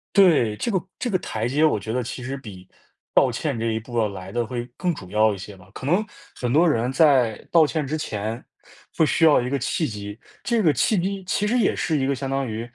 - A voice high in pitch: No, low, 130 Hz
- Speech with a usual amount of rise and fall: No, wide, 6.2 semitones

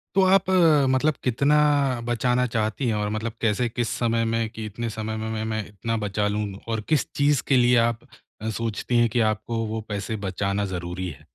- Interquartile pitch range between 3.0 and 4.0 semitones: No, narrow, 2.4 semitones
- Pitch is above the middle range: No, low, 115 Hz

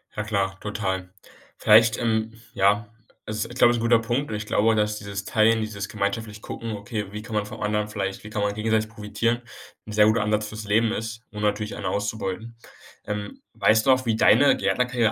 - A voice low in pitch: Yes, low, 110 Hz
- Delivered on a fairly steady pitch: Yes, narrow, 1.5 semitones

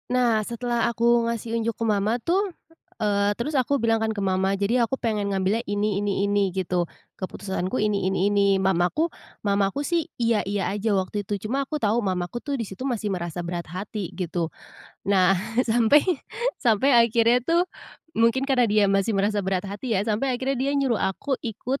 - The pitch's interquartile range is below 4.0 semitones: Yes, average, 3.4 semitones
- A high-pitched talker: Yes, high, 215 Hz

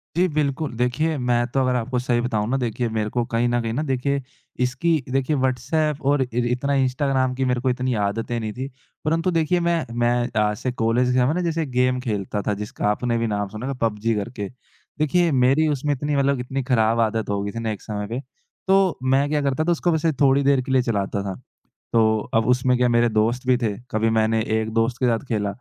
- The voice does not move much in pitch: No, average, 3.6 semitones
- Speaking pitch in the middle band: No, low, 125 Hz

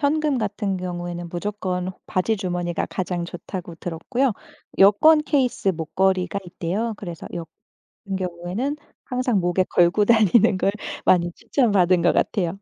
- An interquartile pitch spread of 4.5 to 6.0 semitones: No, average, 3.9 semitones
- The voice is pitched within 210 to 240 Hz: No, medium, 185 Hz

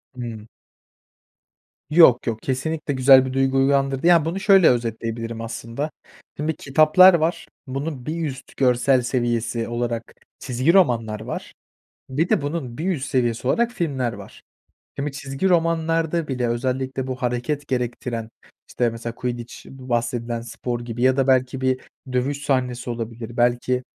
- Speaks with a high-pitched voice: No, low, 130 Hz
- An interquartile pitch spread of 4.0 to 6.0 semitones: No, average, 3.4 semitones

